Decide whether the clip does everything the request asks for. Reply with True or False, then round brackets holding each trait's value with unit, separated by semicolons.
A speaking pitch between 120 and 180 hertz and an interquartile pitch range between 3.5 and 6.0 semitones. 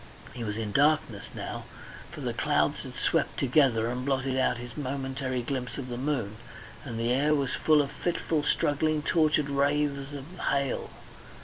False (140 Hz; 2.8 semitones)